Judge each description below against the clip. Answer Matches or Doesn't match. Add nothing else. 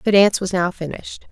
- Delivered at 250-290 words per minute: Doesn't match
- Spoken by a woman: Matches